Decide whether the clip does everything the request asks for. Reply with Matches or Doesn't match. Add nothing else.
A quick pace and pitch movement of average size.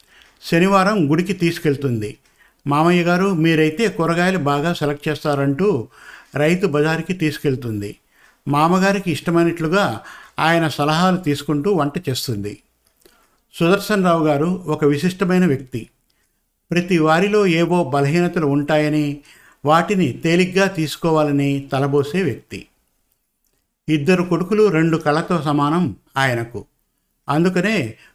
Doesn't match